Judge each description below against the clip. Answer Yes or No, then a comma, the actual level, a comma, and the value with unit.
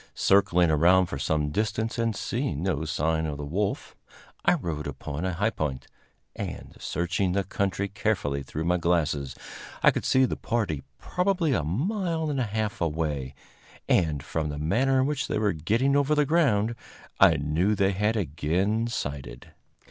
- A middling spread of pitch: No, wide, 6.7 semitones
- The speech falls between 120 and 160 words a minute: No, average, 170 wpm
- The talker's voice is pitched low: Yes, very low, 95 Hz